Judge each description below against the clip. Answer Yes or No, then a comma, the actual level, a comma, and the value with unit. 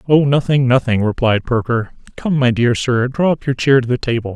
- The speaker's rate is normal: No, fast, 220 wpm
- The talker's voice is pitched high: No, low, 125 Hz